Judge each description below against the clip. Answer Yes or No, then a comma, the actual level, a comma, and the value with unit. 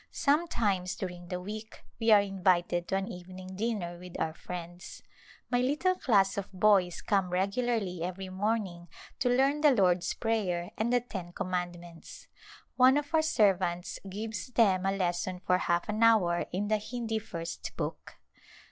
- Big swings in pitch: No, average, 4.0 semitones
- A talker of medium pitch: No, high, 195 Hz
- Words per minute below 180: Yes, average, 160 wpm